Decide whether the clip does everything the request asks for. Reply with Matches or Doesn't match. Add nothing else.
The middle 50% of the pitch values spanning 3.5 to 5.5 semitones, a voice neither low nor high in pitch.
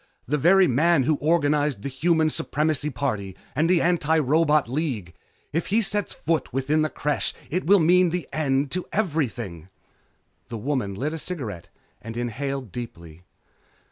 Matches